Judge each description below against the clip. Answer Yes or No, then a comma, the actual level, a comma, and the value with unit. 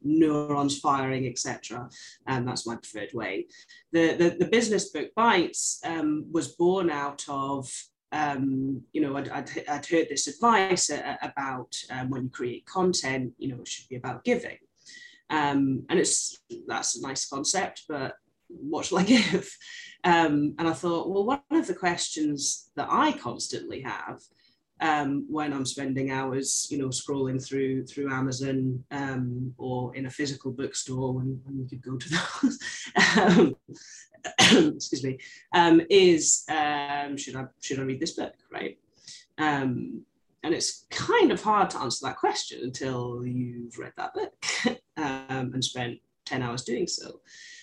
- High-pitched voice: No, medium, 145 Hz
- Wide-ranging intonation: Yes, wide, 6.8 semitones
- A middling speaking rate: Yes, average, 160 wpm